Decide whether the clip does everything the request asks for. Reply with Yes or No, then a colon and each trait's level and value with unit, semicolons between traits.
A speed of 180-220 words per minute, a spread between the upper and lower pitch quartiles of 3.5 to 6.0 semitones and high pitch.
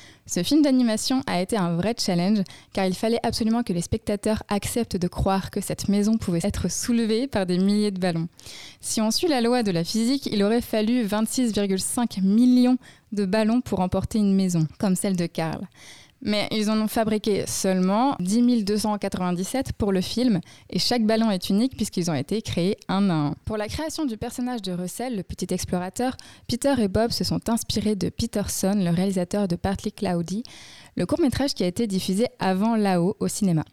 Yes: average, 195 wpm; average, 3.8 semitones; high, 205 Hz